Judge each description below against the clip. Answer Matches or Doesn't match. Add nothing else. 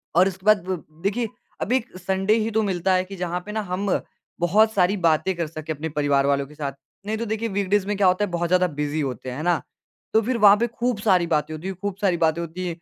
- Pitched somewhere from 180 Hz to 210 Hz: Matches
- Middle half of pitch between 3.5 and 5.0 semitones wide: Matches